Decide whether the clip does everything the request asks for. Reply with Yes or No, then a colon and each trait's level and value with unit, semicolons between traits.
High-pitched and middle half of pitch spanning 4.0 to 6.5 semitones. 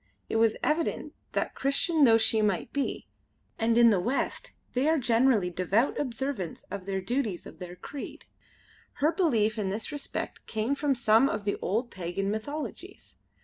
Yes: high, 225 Hz; wide, 5.4 semitones